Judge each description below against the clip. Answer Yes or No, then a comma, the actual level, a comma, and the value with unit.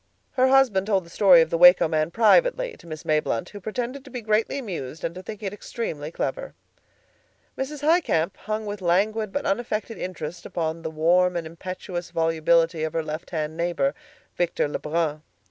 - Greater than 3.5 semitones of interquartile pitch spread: Yes, average, 5.1 semitones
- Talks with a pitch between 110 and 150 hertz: No, medium, 180 Hz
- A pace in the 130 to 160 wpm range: No, average, 180 wpm